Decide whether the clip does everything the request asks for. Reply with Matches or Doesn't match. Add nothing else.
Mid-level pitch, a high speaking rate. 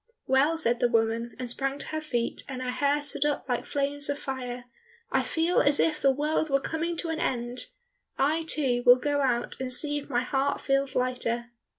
Doesn't match